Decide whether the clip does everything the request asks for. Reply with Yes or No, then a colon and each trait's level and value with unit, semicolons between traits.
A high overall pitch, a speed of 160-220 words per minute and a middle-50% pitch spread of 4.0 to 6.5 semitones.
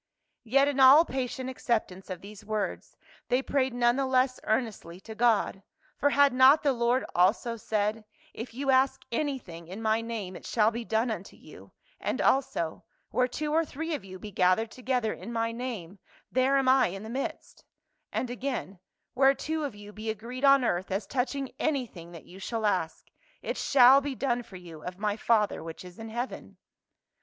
Yes: high, 235 Hz; average, 190 wpm; average, 4.3 semitones